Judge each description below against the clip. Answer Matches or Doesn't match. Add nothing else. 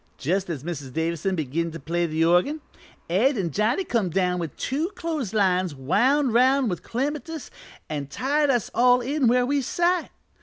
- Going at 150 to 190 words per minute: Matches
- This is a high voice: Matches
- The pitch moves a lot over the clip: Matches